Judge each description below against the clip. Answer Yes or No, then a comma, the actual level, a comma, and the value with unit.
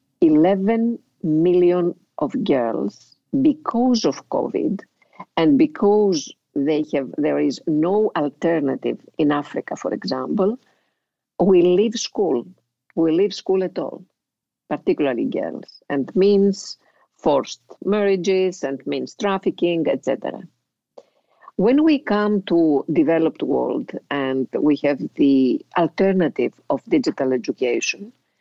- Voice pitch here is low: No, medium, 180 Hz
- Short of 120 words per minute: Yes, slow, 110 wpm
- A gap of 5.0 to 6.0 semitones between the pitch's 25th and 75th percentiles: Yes, wide, 5.6 semitones